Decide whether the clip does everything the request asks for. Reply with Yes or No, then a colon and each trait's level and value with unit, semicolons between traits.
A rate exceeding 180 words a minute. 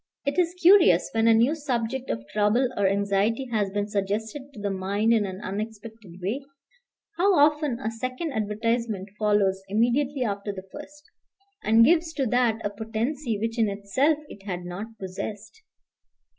No: average, 160 wpm